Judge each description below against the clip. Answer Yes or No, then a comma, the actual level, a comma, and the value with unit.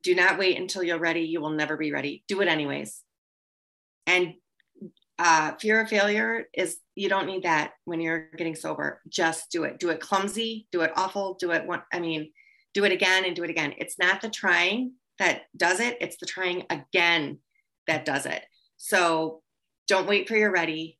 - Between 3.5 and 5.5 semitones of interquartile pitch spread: No, average, 3.1 semitones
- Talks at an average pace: Yes, average, 190 wpm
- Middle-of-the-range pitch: Yes, medium, 180 Hz